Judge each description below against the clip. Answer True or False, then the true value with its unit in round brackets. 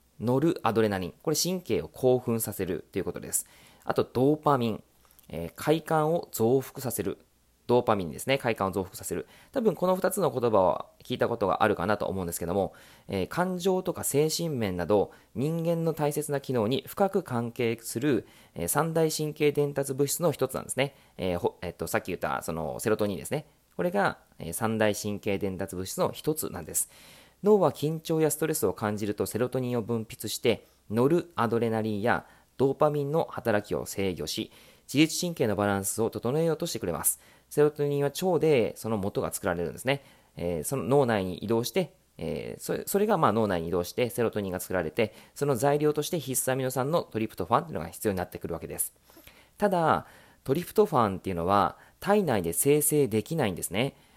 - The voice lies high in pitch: False (125 Hz)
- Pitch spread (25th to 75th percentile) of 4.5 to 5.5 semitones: False (6.8 semitones)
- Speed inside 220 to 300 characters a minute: False (395 characters per minute)